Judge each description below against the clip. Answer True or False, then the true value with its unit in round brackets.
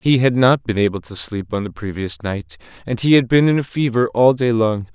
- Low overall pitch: True (115 Hz)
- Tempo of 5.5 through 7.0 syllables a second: False (5.2 syllables/s)